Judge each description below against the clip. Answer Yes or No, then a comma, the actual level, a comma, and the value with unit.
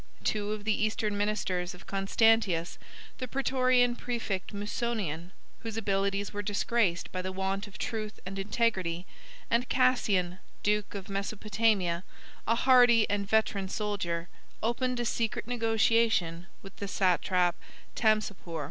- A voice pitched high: Yes, high, 205 Hz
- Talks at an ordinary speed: No, slow, 130 wpm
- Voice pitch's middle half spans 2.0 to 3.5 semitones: Yes, average, 3.1 semitones